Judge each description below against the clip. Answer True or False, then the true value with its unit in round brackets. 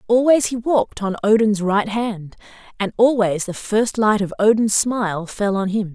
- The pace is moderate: True (180 wpm)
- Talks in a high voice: True (210 Hz)